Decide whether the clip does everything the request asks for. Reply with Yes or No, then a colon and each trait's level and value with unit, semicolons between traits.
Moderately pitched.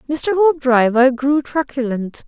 No: very high, 270 Hz